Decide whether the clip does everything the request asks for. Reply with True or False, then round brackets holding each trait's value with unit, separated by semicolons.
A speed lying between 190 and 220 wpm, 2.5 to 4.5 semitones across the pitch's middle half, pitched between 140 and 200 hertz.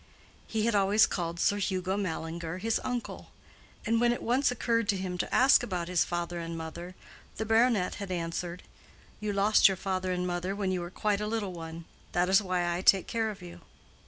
True (205 wpm; 3.4 semitones; 185 Hz)